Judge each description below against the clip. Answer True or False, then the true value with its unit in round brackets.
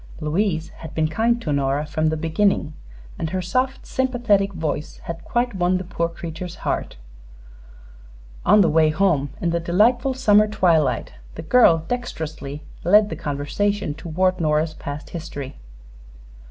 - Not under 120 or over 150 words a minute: True (145 wpm)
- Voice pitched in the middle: True (170 Hz)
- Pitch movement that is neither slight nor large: True (4.8 semitones)